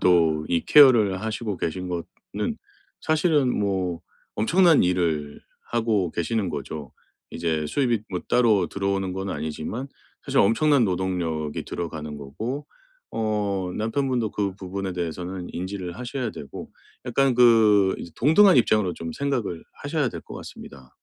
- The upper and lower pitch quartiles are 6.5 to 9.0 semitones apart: No, wide, 5.4 semitones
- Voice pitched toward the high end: No, very low, 95 Hz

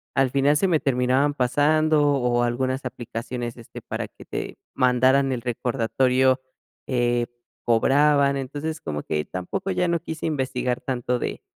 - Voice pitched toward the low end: Yes, low, 130 Hz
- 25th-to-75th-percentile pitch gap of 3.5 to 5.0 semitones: No, average, 2.9 semitones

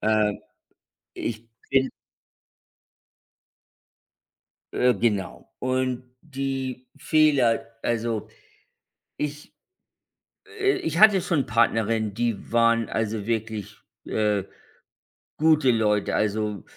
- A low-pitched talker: Yes, low, 115 Hz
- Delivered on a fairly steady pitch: No, average, 3.6 semitones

